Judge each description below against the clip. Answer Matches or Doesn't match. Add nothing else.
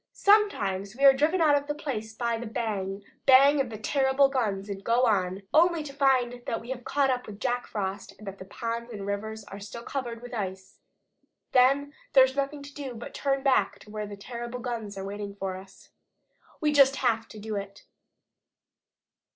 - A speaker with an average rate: Doesn't match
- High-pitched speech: Matches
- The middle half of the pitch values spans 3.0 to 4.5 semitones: Doesn't match